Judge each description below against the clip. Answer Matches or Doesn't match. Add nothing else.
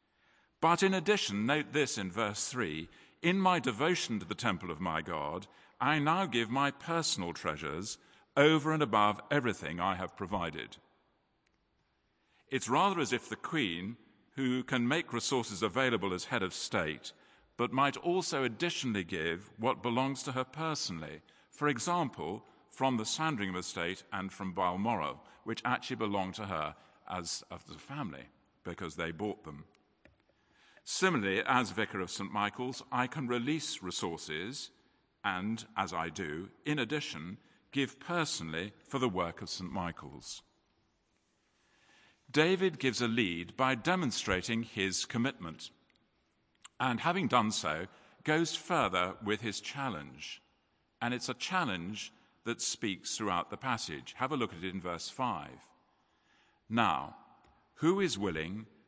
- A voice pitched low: Matches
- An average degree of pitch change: Doesn't match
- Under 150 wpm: Matches